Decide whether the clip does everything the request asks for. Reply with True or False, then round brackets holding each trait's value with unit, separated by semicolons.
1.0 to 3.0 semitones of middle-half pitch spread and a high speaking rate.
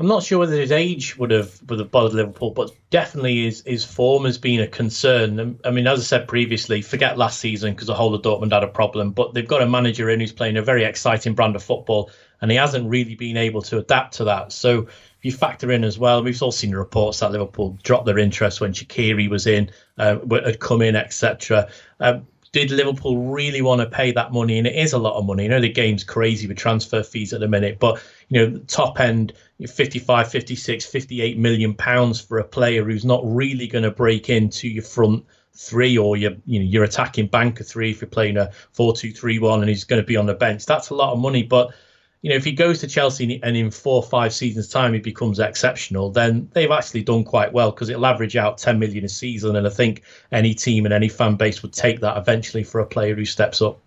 True (2.5 semitones; 240 wpm)